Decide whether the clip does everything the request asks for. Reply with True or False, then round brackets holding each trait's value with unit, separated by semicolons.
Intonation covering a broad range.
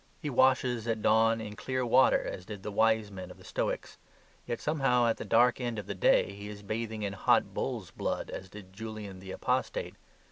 False (2.7 semitones)